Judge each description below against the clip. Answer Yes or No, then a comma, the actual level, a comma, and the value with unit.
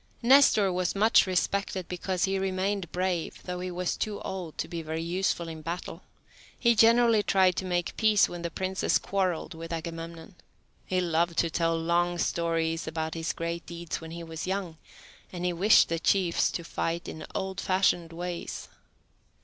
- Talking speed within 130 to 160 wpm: No, average, 175 wpm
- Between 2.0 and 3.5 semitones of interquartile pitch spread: Yes, narrow, 2.4 semitones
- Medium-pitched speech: Yes, medium, 175 Hz